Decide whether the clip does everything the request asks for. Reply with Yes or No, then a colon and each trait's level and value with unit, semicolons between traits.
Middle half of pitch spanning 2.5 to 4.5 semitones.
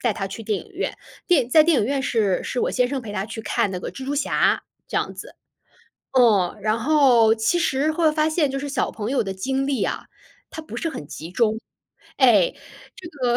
No: average, 5.0 semitones